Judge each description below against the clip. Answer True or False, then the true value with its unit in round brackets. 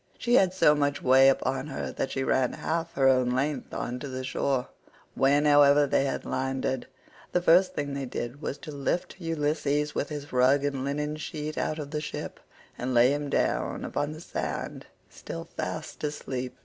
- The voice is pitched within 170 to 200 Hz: False (145 Hz)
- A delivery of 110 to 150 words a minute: False (190 wpm)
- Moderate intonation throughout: False (2.1 semitones)